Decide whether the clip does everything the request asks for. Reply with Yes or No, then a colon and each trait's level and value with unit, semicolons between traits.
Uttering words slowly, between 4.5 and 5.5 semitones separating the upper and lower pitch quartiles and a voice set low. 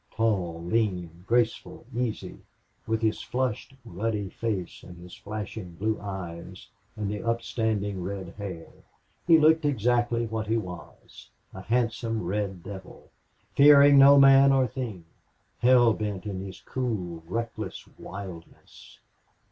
No: slow, 125 wpm; average, 4.1 semitones; low, 110 Hz